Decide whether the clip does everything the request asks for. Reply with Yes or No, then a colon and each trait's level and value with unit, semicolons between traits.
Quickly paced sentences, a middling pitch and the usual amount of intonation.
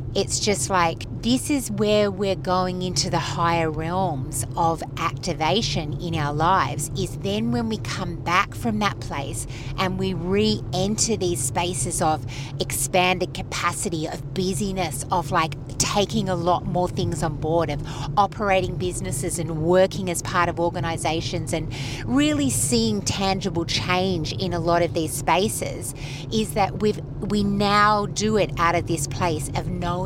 No: average, 155 wpm; medium, 165 Hz; average, 4.9 semitones